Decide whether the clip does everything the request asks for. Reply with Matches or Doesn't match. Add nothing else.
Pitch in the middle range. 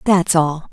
Matches